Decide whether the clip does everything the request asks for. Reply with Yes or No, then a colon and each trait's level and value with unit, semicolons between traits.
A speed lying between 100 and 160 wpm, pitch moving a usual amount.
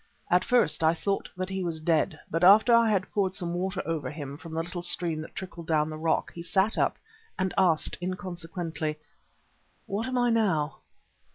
No: average, 190 wpm; average, 3.1 semitones